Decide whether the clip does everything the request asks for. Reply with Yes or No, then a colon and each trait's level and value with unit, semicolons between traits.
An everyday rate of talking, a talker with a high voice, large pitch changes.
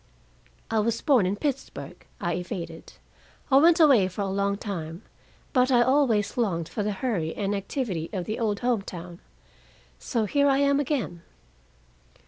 Yes: average, 160 wpm; high, 210 Hz; wide, 5.9 semitones